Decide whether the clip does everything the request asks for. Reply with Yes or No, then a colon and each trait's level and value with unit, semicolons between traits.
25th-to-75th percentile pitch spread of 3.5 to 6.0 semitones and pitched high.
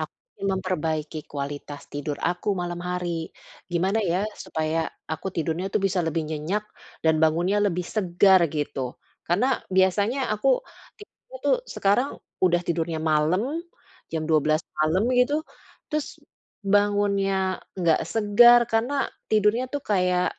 No: average, 4.3 semitones; medium, 180 Hz